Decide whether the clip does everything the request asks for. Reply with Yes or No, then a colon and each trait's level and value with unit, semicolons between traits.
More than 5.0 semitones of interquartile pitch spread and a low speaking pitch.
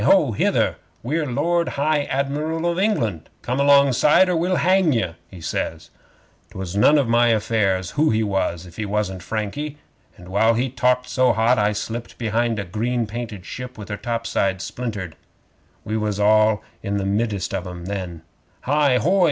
Yes: wide, 5.6 semitones; low, 115 Hz